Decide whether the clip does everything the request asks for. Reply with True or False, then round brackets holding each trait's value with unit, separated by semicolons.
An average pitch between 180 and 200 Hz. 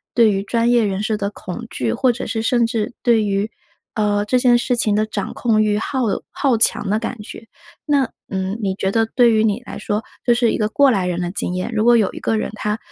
False (220 Hz)